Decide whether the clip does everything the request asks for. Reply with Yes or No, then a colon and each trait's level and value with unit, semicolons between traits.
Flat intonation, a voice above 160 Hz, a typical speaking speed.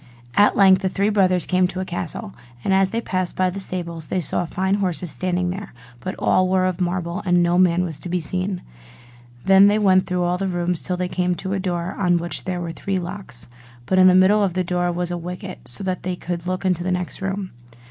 No: narrow, 1.3 semitones; medium, 185 Hz; fast, 240 wpm